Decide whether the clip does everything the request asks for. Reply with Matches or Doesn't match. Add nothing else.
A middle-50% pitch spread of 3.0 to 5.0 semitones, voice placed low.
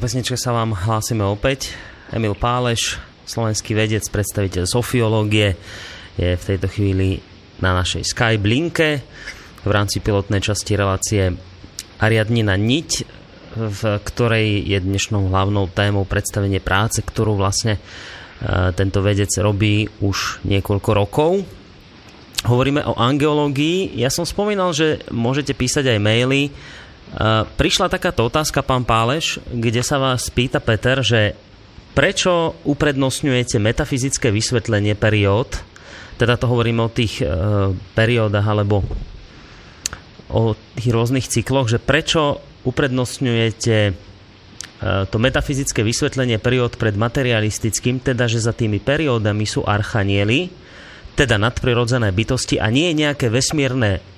Matches